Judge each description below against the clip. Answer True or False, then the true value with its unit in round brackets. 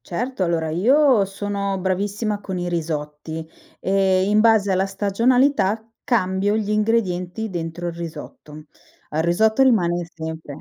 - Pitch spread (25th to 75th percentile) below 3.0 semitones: False (3.8 semitones)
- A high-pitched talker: True (195 Hz)